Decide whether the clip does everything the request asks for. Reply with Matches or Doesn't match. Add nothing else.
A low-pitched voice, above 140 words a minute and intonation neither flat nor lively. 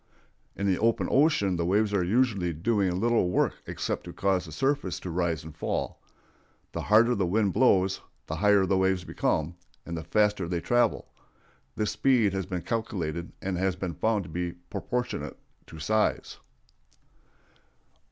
Matches